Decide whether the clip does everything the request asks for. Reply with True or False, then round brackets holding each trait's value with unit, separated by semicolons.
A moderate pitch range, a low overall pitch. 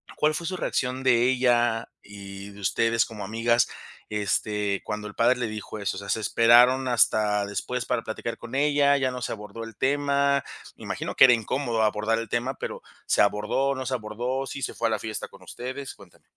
True (3.4 semitones; 115 Hz)